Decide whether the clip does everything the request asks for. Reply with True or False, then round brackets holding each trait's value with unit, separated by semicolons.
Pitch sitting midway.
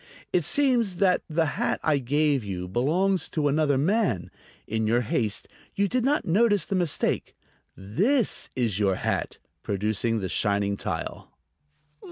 True (145 Hz)